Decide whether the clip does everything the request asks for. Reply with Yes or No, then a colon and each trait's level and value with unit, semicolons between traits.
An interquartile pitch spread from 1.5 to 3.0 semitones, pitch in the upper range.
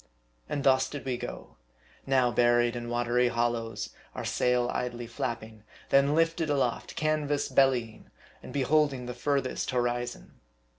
No: narrow, 2.5 semitones; low, 125 Hz